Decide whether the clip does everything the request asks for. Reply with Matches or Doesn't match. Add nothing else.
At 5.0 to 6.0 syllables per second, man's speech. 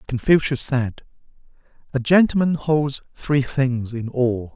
Doesn't match